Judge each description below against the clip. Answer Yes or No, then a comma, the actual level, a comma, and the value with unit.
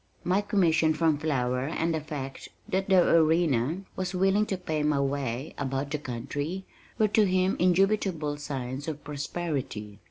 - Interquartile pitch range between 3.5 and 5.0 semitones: Yes, average, 4.7 semitones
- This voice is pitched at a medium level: Yes, medium, 155 Hz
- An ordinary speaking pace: Yes, average, 155 wpm